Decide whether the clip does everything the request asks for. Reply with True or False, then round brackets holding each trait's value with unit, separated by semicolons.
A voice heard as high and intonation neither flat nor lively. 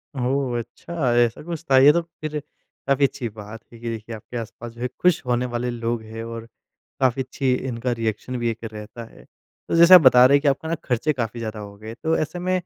False (125 Hz; 3.6 semitones)